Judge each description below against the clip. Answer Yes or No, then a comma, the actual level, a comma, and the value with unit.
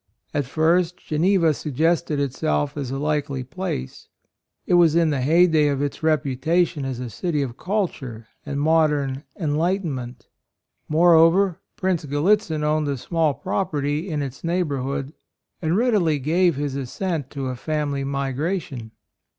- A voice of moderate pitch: Yes, medium, 150 Hz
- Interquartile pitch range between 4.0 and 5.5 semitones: No, average, 3.6 semitones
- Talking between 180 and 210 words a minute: No, average, 140 wpm